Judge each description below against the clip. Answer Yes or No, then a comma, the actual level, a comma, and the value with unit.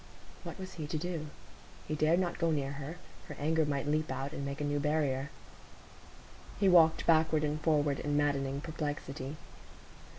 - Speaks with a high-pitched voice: No, medium, 150 Hz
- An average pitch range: No, narrow, 2.0 semitones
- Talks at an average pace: Yes, average, 170 wpm